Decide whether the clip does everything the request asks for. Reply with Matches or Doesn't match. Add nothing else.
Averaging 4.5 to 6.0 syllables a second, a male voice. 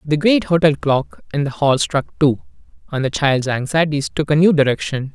Matches